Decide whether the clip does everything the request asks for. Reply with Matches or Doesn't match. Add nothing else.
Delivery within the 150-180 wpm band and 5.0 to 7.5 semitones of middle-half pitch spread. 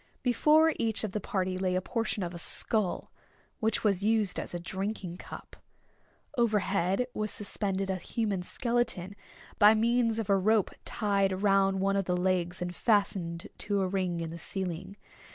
Doesn't match